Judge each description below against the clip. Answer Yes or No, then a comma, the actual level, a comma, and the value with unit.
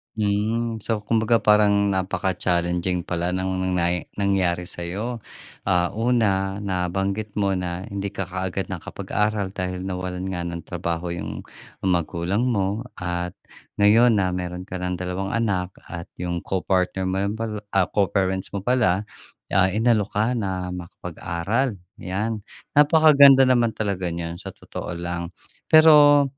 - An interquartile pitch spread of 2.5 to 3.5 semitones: Yes, average, 3.0 semitones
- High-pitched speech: No, very low, 95 Hz